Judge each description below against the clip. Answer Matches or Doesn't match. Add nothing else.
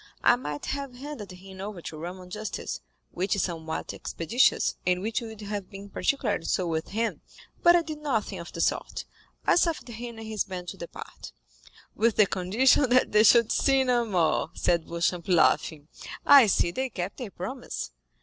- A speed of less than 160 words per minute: Doesn't match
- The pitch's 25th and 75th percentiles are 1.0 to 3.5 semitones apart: Doesn't match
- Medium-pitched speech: Doesn't match